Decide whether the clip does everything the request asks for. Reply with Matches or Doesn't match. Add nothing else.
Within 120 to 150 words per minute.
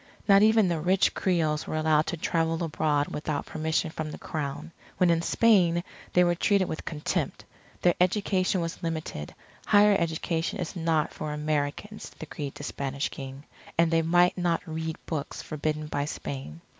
Doesn't match